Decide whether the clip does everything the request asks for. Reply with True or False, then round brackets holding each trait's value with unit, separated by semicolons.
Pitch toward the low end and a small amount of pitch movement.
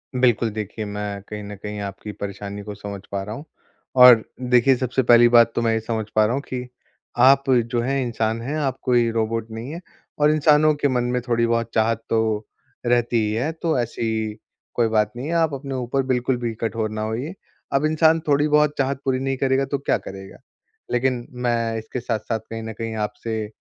False (120 Hz; 3.2 semitones)